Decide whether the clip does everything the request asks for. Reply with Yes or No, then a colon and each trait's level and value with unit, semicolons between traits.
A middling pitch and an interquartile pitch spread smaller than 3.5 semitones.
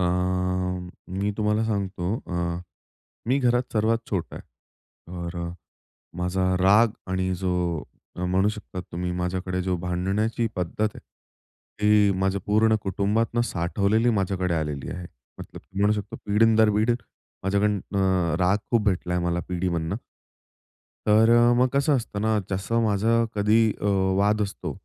No: very low, 95 Hz; average, 2.9 semitones